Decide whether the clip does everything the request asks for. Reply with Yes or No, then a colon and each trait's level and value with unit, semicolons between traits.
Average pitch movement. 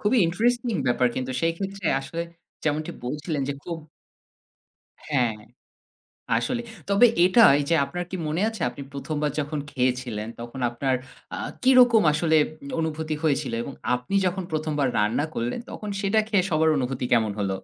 No: wide, 6.6 semitones